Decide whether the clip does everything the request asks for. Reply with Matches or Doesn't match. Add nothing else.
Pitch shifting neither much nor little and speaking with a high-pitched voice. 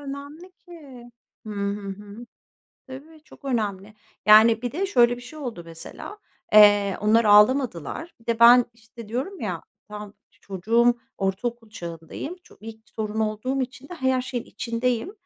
Matches